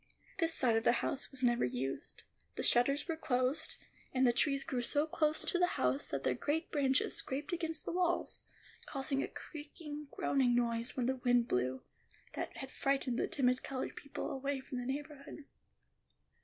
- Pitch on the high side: Yes, very high, 270 Hz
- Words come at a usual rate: Yes, average, 180 wpm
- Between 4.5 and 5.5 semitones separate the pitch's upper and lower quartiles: No, average, 3.3 semitones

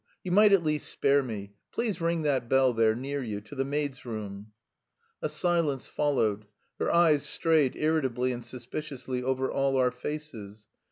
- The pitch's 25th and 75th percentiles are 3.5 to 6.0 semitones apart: Yes, average, 4.2 semitones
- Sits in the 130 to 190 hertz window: Yes, low, 135 Hz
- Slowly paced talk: No, average, 165 wpm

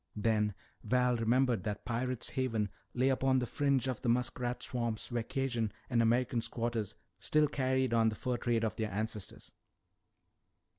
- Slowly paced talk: No, average, 155 wpm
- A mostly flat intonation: Yes, narrow, 2.3 semitones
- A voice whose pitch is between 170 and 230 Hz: No, low, 120 Hz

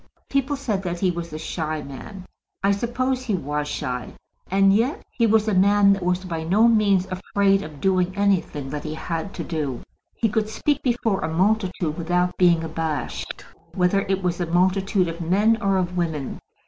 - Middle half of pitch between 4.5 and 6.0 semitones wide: No, average, 3.6 semitones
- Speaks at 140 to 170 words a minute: No, average, 185 wpm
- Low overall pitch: No, medium, 185 Hz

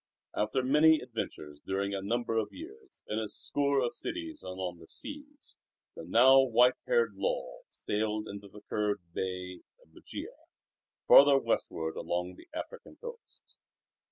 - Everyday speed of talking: Yes, average, 150 wpm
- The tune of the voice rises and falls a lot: Yes, wide, 7.7 semitones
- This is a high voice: No, low, 110 Hz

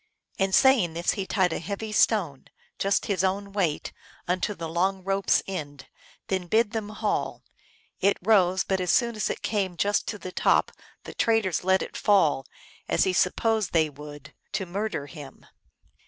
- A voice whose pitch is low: No, high, 190 Hz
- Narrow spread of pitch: No, average, 3.3 semitones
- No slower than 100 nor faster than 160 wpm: No, average, 175 wpm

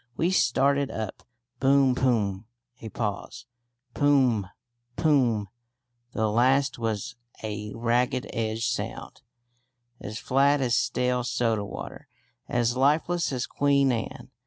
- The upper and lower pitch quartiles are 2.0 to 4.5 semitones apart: Yes, average, 3.6 semitones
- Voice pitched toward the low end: Yes, low, 125 Hz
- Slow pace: Yes, slow, 120 wpm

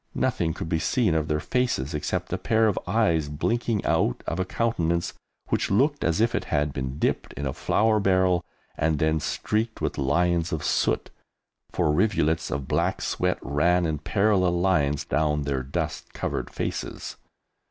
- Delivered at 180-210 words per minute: No, average, 170 wpm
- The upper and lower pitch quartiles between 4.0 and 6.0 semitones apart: Yes, wide, 5.5 semitones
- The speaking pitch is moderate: No, very low, 85 Hz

